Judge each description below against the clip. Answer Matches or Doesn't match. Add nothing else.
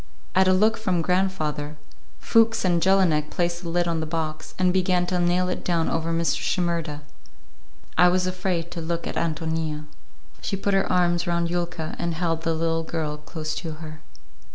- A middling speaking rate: Matches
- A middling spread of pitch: Doesn't match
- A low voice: Doesn't match